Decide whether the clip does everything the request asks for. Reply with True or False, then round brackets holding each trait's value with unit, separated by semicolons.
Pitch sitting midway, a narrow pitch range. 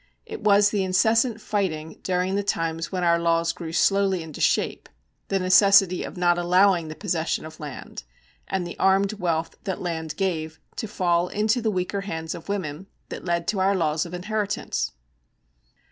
False (180 Hz; 3.2 semitones)